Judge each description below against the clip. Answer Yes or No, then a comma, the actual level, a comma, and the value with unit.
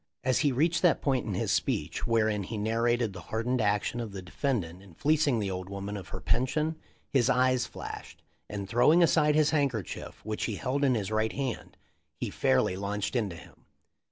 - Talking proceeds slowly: No, average, 195 wpm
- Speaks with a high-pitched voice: No, low, 115 Hz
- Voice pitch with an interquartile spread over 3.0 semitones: Yes, average, 4.9 semitones